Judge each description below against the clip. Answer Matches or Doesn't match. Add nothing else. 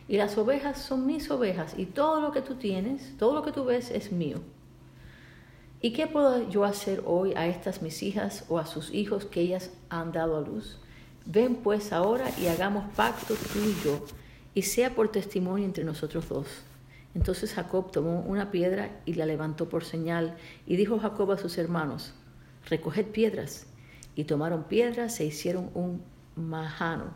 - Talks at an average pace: Matches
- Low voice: Doesn't match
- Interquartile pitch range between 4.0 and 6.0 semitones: Matches